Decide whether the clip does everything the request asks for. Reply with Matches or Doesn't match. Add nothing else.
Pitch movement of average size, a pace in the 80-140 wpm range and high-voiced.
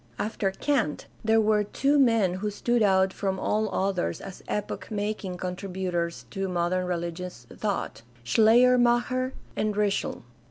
Matches